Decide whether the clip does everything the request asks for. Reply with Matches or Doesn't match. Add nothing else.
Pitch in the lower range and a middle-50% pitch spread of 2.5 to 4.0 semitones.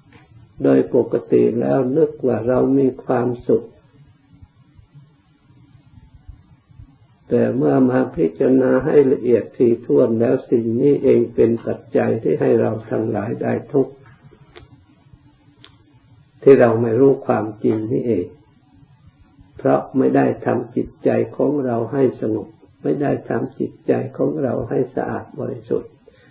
Matches